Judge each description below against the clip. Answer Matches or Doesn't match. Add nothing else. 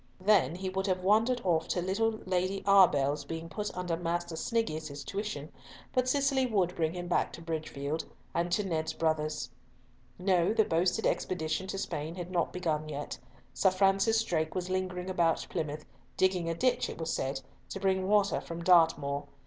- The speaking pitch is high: Doesn't match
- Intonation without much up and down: Doesn't match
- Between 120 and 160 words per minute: Doesn't match